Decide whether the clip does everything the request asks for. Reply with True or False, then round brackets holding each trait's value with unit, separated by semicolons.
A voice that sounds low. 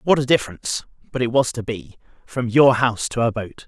True (120 Hz)